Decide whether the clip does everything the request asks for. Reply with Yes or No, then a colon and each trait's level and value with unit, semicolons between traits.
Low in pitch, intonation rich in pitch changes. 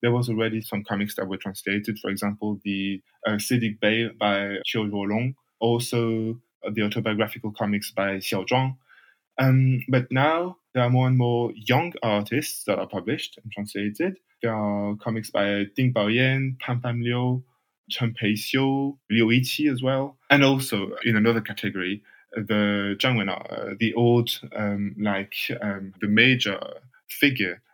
No: low, 115 Hz; average, 3.5 semitones